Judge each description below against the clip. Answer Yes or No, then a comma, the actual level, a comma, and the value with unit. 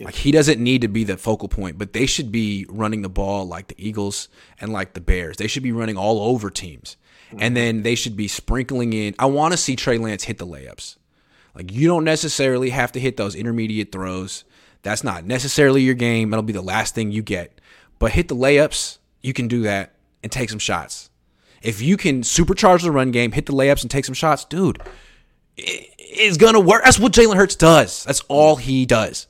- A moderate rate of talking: No, fast, 225 wpm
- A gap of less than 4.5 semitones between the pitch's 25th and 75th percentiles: No, average, 5.2 semitones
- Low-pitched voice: Yes, low, 120 Hz